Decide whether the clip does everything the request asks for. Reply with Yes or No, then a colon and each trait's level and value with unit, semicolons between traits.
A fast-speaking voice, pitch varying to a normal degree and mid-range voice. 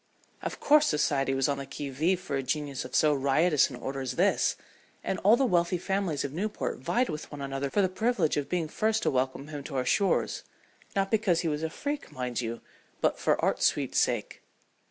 No: fast, 215 wpm; wide, 5.8 semitones; medium, 155 Hz